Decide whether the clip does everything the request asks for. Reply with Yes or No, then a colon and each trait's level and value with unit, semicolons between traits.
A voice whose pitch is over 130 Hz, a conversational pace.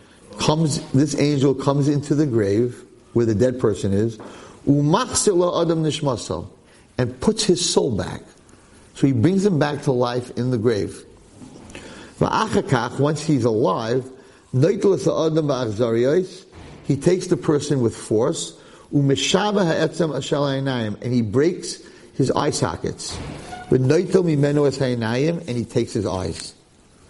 No: medium, 140 Hz; slow, 105 wpm